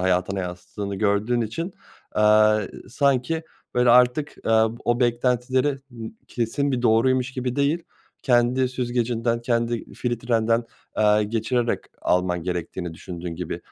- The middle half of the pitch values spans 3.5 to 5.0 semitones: No, average, 2.8 semitones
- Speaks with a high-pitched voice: No, low, 120 Hz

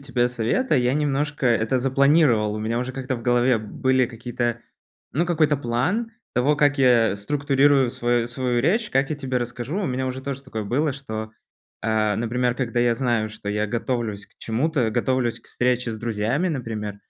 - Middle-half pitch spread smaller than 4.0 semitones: Yes, average, 3.1 semitones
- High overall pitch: No, low, 125 Hz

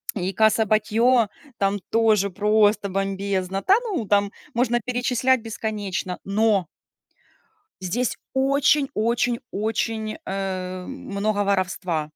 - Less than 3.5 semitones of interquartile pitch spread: Yes, average, 3.0 semitones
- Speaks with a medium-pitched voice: No, high, 210 Hz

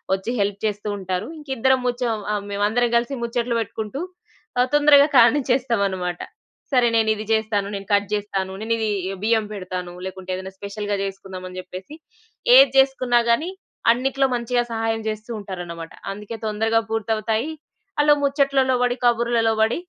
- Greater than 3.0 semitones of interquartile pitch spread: Yes, average, 3.5 semitones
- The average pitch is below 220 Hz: No, high, 225 Hz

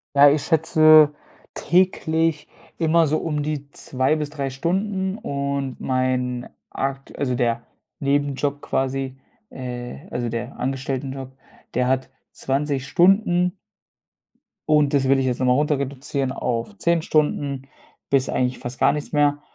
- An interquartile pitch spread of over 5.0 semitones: No, average, 2.8 semitones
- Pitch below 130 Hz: No, medium, 140 Hz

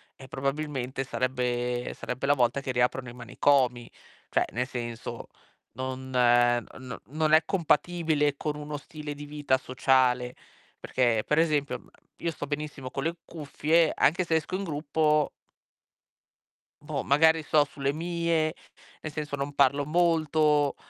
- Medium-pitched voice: Yes, medium, 145 Hz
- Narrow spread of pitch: No, average, 3.2 semitones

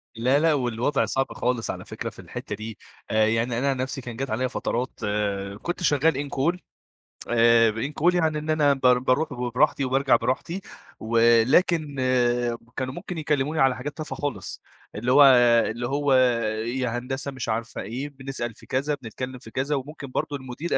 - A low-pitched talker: Yes, low, 130 Hz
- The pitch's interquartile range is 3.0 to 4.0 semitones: Yes, average, 3.3 semitones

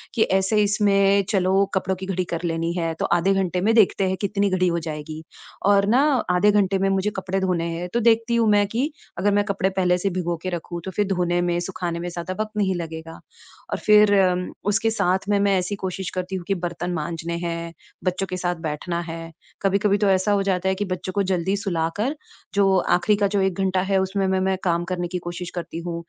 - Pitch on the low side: No, medium, 185 Hz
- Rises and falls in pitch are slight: Yes, narrow, 2.3 semitones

